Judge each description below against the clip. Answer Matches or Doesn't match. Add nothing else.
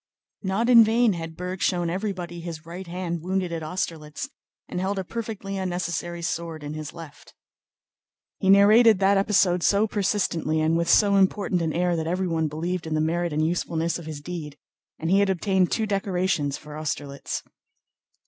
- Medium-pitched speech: Matches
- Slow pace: Doesn't match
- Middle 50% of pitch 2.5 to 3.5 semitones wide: Matches